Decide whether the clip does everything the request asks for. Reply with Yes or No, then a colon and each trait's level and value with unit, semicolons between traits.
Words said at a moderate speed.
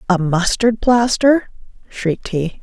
No: slow, 115 wpm